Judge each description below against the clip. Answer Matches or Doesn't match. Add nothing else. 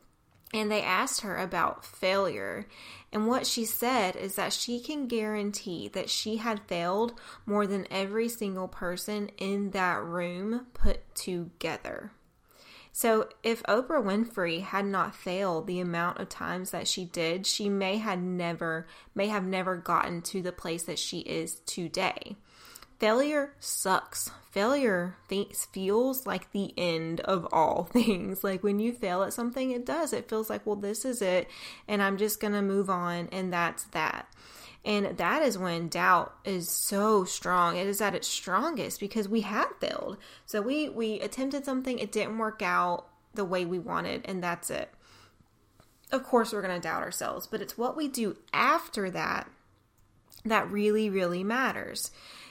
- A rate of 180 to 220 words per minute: Doesn't match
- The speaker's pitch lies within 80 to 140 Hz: Doesn't match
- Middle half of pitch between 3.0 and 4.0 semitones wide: Matches